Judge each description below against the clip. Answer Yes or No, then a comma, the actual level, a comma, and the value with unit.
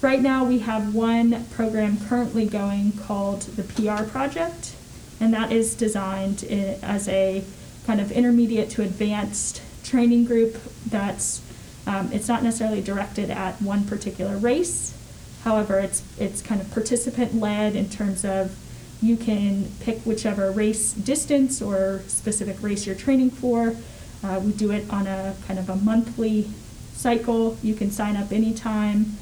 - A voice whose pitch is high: Yes, high, 215 Hz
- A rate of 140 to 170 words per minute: Yes, average, 150 wpm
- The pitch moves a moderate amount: No, narrow, 2.3 semitones